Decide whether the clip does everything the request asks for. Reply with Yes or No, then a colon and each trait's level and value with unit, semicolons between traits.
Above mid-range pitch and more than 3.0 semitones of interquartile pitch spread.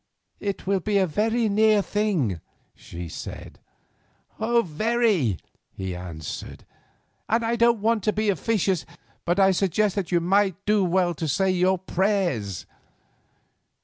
Yes: high, 195 Hz; average, 4.0 semitones